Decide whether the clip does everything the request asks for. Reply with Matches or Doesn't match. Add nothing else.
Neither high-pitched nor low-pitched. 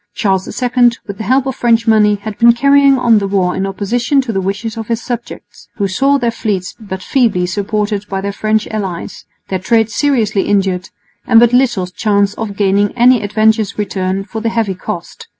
Doesn't match